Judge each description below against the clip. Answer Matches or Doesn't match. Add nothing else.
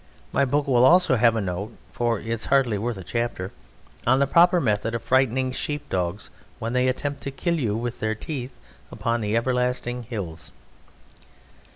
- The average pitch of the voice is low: Matches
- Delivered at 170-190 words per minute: Matches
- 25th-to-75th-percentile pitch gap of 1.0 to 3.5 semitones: Matches